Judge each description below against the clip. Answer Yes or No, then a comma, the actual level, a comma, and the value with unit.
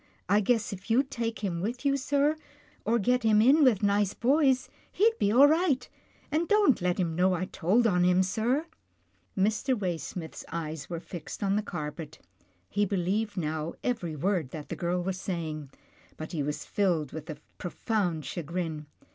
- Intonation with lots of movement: Yes, wide, 6.0 semitones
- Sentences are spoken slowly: No, average, 180 wpm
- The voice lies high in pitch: Yes, high, 195 Hz